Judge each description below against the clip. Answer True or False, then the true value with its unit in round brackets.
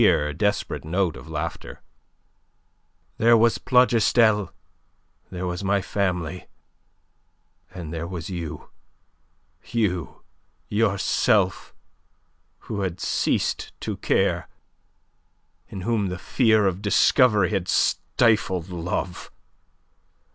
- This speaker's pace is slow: True (105 wpm)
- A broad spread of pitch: False (3.7 semitones)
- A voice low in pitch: True (95 Hz)